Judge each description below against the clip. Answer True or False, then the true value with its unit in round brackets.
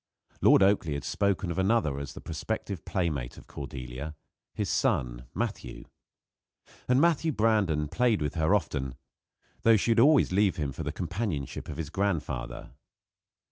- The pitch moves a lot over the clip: True (6.7 semitones)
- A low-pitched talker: True (85 Hz)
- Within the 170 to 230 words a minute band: False (150 wpm)